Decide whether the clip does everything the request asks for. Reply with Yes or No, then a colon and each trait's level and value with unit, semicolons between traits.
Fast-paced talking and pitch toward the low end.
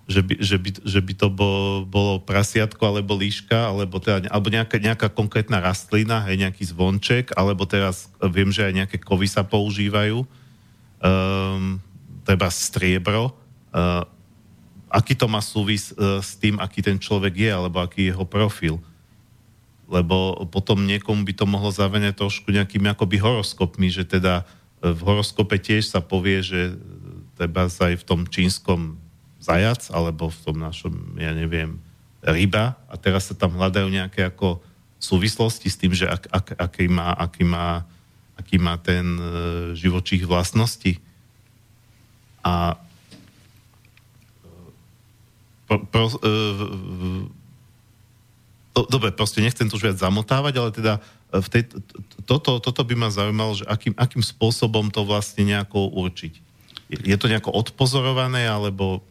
No: average, 145 wpm; low, 100 Hz